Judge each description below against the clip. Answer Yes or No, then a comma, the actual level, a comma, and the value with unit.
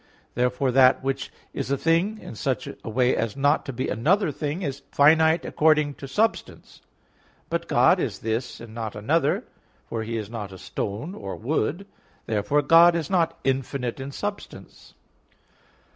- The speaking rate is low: No, average, 160 wpm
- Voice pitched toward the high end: No, low, 135 Hz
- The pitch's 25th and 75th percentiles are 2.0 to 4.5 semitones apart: No, wide, 5.5 semitones